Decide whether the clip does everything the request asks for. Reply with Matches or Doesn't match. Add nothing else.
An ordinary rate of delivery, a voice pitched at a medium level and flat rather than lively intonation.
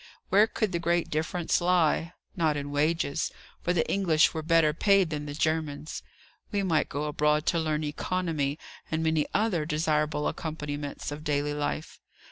Matches